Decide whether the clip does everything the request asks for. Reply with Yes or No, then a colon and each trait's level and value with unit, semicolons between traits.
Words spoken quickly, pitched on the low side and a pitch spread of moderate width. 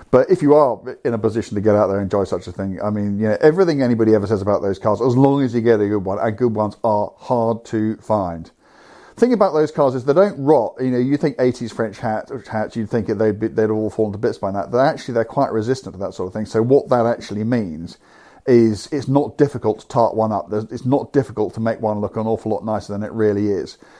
Yes: fast, 270 wpm; low, 110 Hz; average, 3.4 semitones